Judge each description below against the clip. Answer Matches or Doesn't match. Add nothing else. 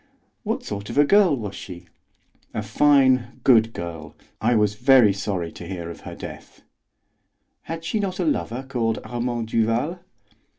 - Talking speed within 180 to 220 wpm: Doesn't match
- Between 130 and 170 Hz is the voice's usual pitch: Doesn't match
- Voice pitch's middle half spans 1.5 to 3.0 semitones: Doesn't match